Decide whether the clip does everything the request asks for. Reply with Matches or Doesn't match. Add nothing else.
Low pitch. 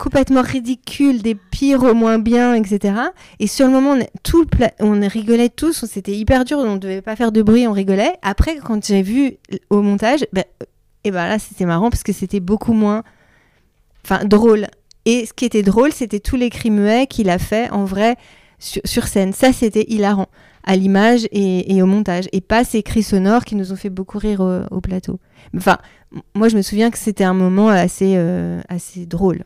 Doesn't match